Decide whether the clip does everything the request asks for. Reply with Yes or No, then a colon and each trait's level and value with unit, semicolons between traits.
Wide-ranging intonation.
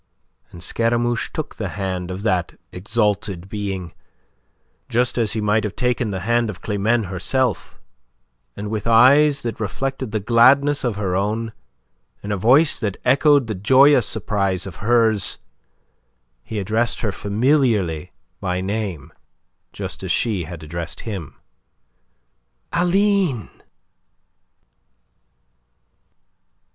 No: average, 3.9 semitones